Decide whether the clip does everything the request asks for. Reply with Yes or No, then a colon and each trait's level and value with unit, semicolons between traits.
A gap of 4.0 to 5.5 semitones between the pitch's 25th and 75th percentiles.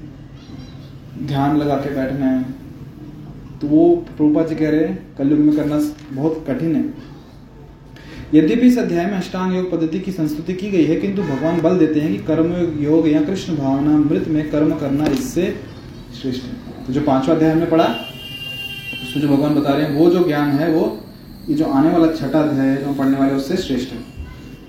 No: average, 3.0 semitones